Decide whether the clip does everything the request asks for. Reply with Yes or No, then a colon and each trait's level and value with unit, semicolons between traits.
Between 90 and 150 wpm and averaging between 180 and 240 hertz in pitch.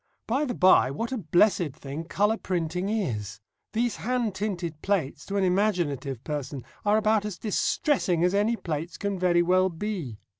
No: average, 165 wpm; medium, 185 Hz